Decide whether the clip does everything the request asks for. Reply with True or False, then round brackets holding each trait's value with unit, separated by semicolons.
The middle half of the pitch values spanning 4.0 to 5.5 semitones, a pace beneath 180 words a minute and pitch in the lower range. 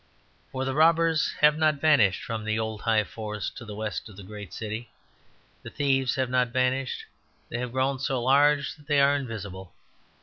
False (4.4 semitones; 190 wpm; 125 Hz)